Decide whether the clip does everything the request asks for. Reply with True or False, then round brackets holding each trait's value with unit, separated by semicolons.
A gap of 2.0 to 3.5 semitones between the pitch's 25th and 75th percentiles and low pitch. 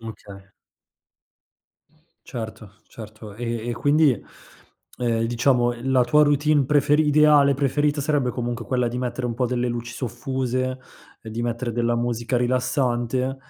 True (2.5 semitones; 125 Hz)